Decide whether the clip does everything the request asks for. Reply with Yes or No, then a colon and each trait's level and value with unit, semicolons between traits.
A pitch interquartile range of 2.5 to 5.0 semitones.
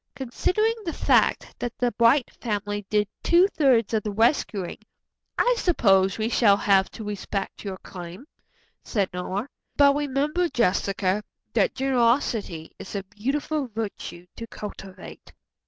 No: wide, 5.4 semitones